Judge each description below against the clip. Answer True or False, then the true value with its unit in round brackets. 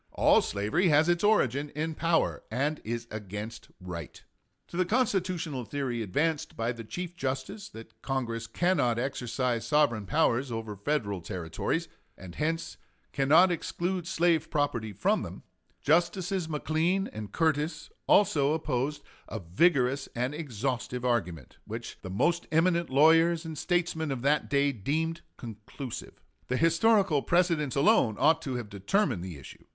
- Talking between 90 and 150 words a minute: True (140 wpm)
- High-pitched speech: False (145 Hz)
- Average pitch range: False (6.1 semitones)